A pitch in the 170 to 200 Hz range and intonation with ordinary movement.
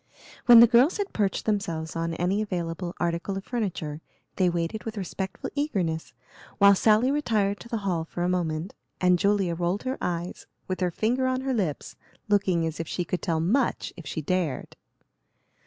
Yes: medium, 185 Hz; average, 4.3 semitones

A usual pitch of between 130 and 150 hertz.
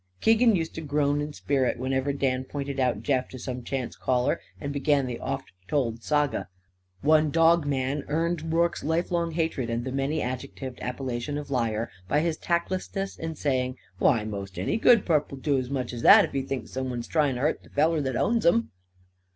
Yes: medium, 140 Hz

